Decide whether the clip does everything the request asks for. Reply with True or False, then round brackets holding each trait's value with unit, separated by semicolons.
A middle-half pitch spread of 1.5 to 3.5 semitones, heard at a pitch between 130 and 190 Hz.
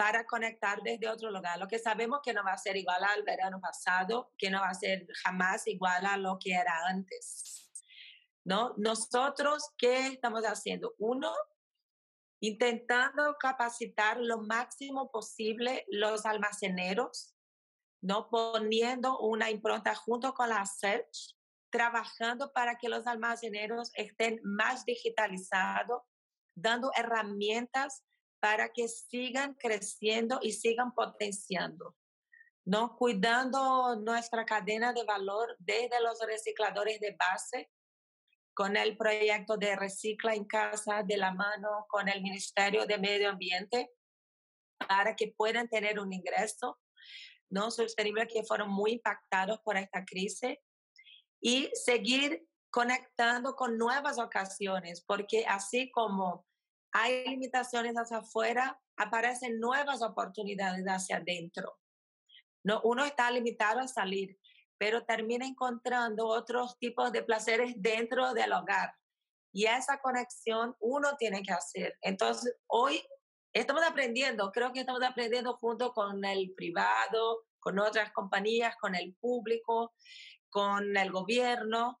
False (2.9 semitones; 230 Hz)